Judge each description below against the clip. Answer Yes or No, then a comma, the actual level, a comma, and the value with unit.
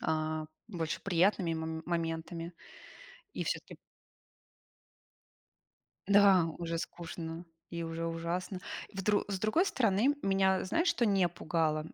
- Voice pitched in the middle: Yes, medium, 175 Hz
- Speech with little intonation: No, average, 3.1 semitones